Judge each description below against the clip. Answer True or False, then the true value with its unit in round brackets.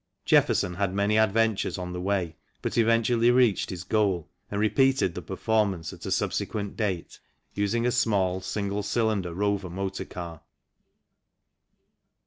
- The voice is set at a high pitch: False (100 Hz)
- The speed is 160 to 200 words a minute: False (135 wpm)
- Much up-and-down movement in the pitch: False (3.1 semitones)